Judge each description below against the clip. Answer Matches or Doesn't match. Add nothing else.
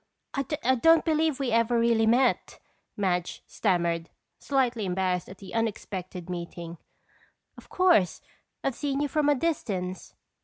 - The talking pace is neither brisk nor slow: Doesn't match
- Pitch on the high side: Matches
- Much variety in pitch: Matches